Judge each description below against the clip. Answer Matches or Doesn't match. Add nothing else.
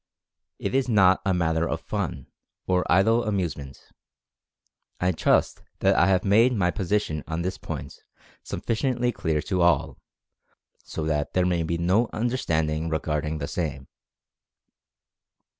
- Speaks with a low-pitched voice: Matches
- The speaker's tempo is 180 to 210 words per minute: Doesn't match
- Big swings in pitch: Doesn't match